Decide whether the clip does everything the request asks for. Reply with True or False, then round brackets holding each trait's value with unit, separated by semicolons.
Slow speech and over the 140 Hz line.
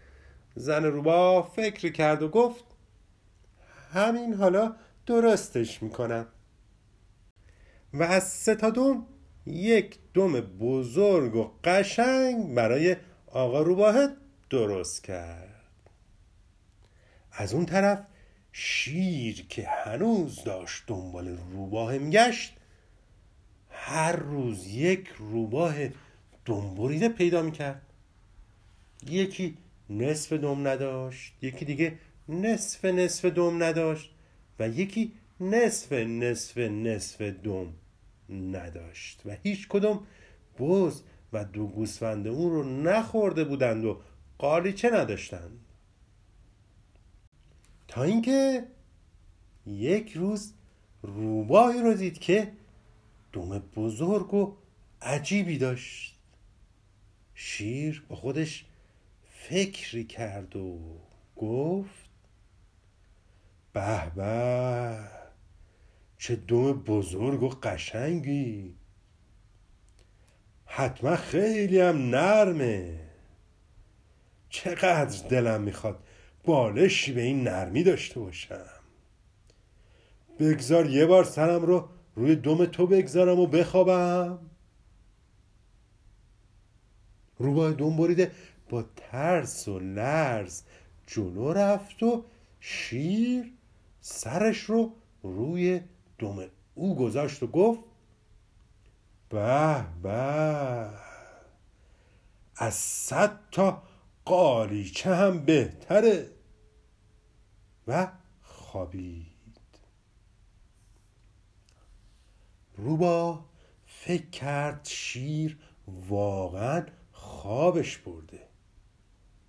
False (80 wpm; 115 Hz)